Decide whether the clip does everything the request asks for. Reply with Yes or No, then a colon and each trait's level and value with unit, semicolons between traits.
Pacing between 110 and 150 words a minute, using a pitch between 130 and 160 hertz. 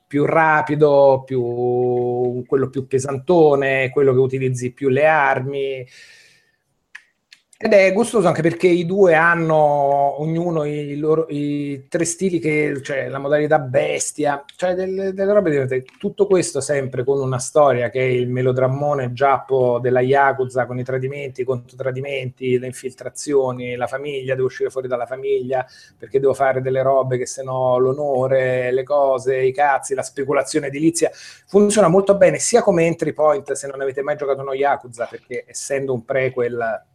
No: average, 160 wpm; medium, 140 Hz